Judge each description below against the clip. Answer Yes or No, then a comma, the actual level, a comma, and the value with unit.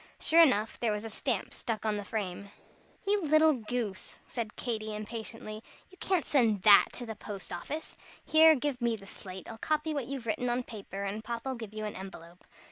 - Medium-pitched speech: No, high, 225 Hz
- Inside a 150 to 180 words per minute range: No, average, 200 wpm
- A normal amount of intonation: Yes, average, 4.1 semitones